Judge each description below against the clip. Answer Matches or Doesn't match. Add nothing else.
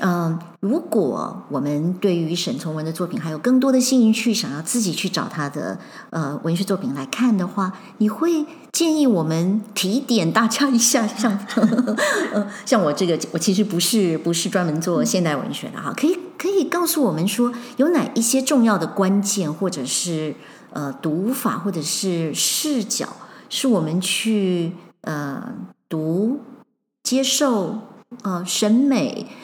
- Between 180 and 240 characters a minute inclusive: Matches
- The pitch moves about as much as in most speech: Doesn't match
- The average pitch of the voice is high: Matches